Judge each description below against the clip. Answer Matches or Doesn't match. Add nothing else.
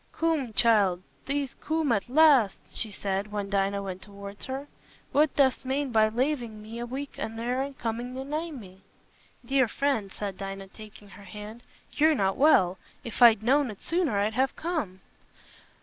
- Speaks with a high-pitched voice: Matches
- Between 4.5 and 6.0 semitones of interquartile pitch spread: Matches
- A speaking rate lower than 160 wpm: Doesn't match